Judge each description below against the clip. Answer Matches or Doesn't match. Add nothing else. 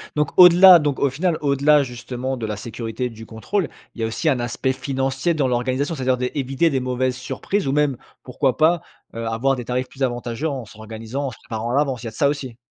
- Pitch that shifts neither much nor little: Matches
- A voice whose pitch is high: Doesn't match